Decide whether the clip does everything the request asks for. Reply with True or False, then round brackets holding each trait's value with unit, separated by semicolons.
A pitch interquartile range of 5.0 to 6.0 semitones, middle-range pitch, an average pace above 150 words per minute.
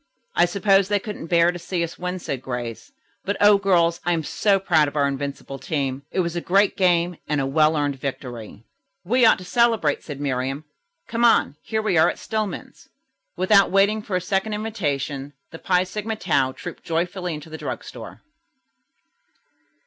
True (5.3 semitones; 175 Hz; 185 wpm)